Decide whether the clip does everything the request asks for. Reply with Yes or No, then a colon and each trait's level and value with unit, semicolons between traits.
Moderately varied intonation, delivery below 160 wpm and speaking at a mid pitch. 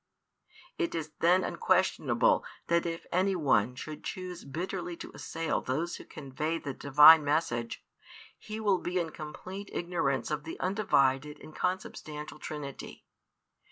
Yes: average, 3.8 semitones; slow, 135 wpm; medium, 160 Hz